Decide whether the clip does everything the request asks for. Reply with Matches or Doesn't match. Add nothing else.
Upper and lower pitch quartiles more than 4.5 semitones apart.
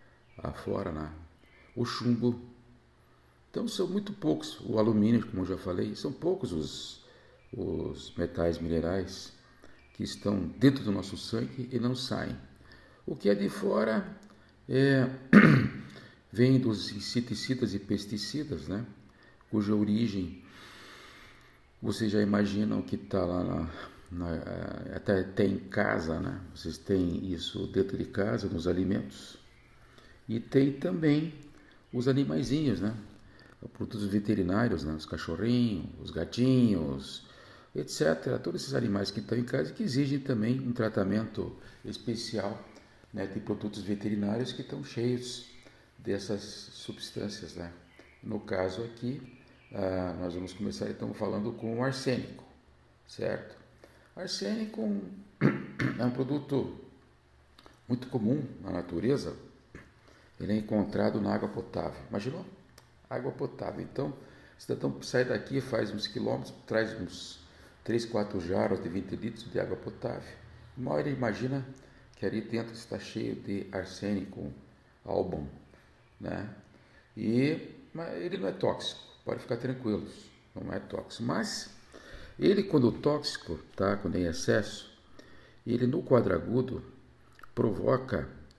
Matches